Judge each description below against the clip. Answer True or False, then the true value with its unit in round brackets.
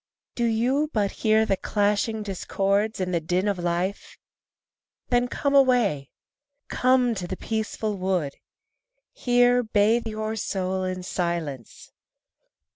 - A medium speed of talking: False (120 wpm)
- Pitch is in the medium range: False (205 Hz)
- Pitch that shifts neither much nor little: True (4.0 semitones)